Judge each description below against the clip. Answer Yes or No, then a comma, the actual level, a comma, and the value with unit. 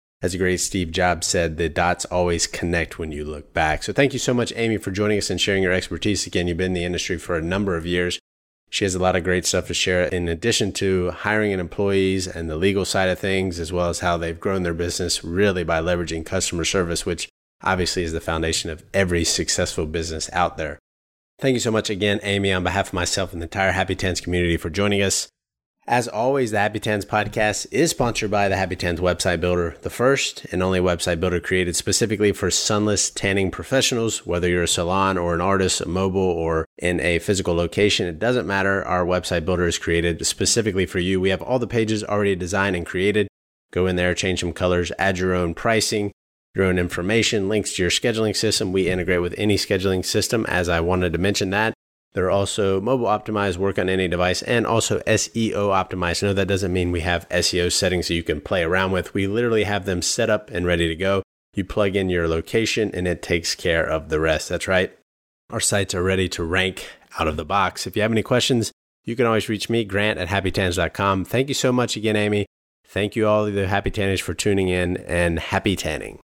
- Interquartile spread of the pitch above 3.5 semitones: No, average, 2.7 semitones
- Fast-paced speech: Yes, fast, 225 wpm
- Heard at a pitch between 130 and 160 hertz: No, very low, 95 Hz